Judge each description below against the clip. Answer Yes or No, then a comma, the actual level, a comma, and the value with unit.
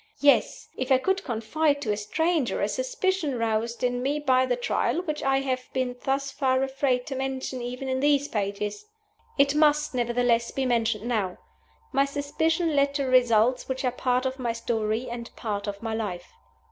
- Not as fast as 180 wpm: No, average, 185 wpm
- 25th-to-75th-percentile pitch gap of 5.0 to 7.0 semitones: No, average, 3.3 semitones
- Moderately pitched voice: No, very high, 255 Hz